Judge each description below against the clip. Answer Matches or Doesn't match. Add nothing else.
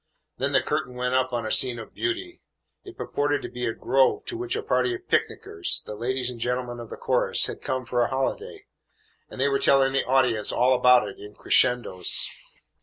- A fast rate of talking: Matches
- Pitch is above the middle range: Doesn't match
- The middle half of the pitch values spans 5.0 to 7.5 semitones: Doesn't match